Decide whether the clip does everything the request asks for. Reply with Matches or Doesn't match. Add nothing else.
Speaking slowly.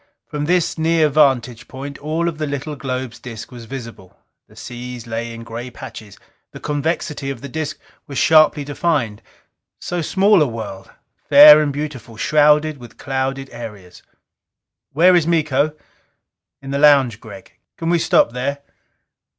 Doesn't match